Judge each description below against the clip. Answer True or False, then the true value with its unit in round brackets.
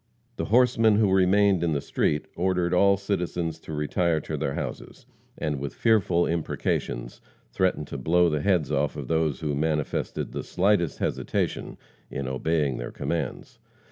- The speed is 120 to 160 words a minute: True (150 wpm)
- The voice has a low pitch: True (85 Hz)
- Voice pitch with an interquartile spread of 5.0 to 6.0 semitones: False (4.1 semitones)